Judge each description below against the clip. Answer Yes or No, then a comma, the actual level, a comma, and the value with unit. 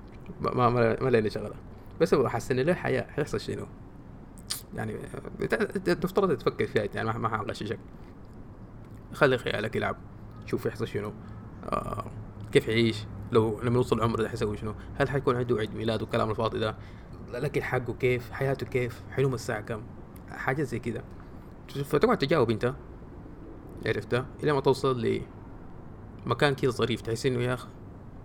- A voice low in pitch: Yes, low, 115 Hz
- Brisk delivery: Yes, fast, 145 wpm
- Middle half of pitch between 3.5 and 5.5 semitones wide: No, average, 2.9 semitones